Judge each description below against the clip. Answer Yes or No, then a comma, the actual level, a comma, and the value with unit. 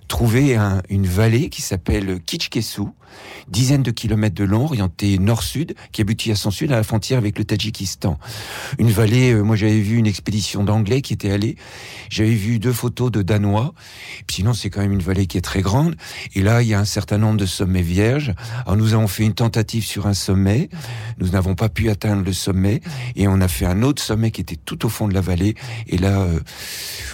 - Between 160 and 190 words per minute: No, fast, 220 wpm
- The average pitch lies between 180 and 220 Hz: No, low, 110 Hz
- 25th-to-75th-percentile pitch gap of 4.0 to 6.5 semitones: No, average, 3.0 semitones